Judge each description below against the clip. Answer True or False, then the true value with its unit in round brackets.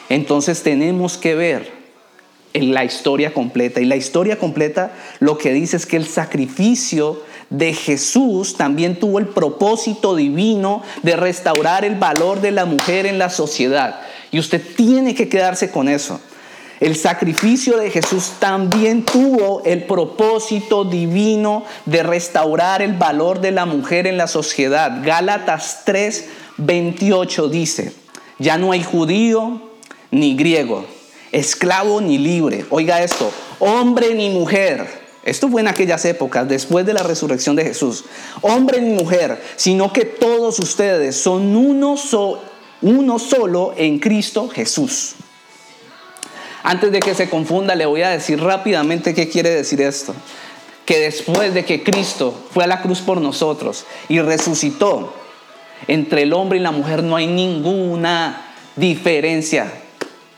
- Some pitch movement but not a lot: True (4.7 semitones)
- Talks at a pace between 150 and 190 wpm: False (140 wpm)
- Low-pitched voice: False (180 Hz)